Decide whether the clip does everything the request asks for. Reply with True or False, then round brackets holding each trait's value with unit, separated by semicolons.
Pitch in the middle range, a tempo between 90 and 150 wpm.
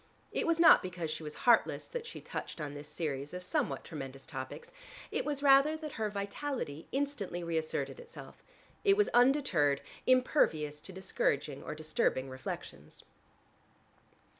True (180 Hz; 145 wpm)